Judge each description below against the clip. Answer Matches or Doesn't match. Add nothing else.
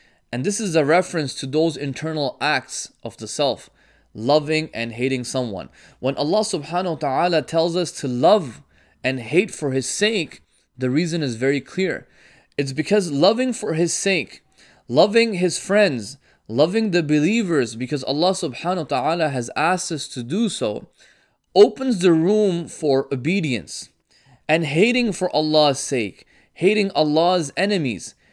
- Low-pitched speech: Doesn't match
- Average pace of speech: Matches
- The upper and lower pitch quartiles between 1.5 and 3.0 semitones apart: Doesn't match